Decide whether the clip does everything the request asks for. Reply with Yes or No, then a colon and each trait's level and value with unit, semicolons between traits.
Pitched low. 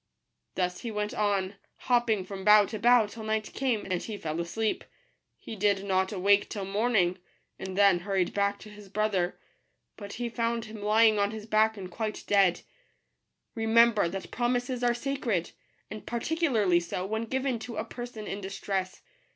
No: high, 210 Hz